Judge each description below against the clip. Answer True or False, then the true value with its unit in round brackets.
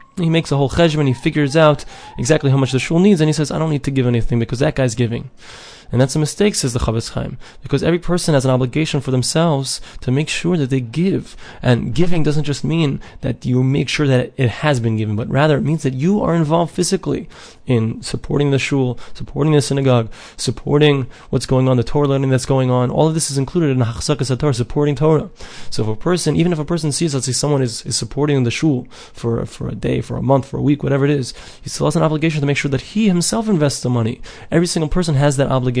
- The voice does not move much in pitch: False (3.5 semitones)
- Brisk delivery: True (255 wpm)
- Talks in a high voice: False (140 Hz)